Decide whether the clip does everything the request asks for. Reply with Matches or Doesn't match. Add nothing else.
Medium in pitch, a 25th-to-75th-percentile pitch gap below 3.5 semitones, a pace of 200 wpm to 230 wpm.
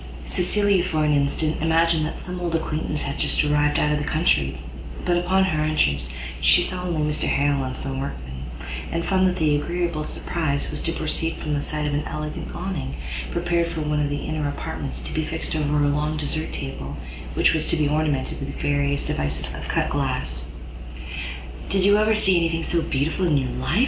Matches